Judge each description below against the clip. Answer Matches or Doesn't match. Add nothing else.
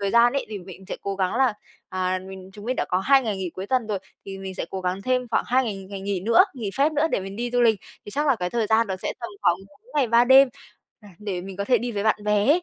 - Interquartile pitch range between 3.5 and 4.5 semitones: Matches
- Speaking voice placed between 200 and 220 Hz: Matches